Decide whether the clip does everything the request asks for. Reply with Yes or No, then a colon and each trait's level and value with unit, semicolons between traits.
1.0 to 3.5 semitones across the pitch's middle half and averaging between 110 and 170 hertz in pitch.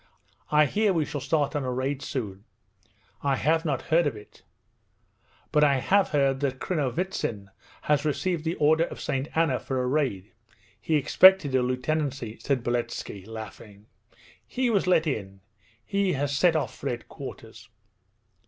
No: average, 4.0 semitones; medium, 140 Hz